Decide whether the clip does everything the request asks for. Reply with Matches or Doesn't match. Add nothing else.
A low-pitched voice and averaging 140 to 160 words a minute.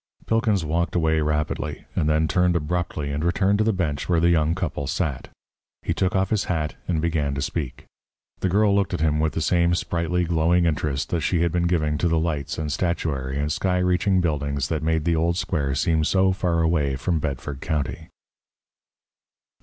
Doesn't match